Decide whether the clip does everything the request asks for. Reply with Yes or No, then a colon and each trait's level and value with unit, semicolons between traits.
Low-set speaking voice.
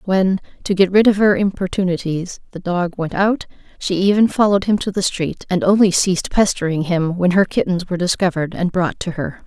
No: medium, 185 Hz